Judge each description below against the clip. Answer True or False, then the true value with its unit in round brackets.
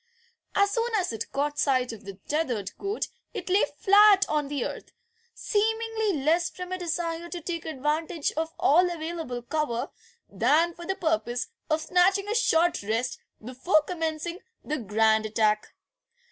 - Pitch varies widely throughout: True (5.8 semitones)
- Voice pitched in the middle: False (320 Hz)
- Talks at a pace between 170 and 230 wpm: False (155 wpm)